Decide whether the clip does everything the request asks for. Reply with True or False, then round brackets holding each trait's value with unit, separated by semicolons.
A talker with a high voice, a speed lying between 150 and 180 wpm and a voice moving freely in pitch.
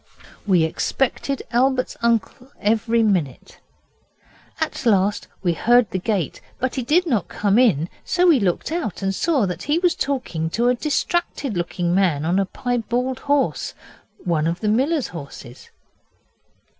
True (225 Hz; 155 wpm; 6.7 semitones)